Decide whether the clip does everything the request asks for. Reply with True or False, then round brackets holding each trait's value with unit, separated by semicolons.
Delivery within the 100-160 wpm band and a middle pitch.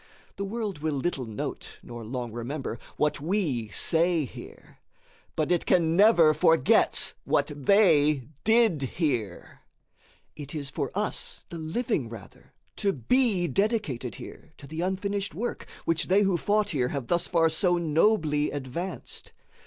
True (145 wpm; 160 Hz)